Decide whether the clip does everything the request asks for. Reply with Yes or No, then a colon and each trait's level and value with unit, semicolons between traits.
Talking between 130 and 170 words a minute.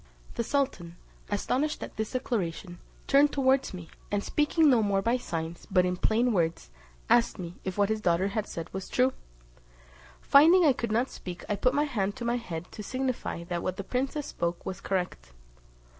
No: average, 185 wpm